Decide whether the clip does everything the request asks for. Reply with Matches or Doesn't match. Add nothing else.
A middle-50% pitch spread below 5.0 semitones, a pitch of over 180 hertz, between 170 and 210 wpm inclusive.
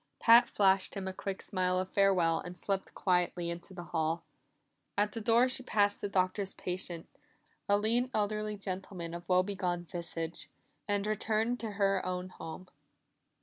Doesn't match